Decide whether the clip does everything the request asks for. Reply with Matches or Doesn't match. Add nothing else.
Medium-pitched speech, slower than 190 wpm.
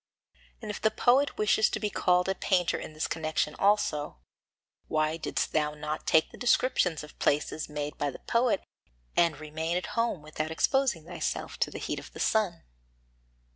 Matches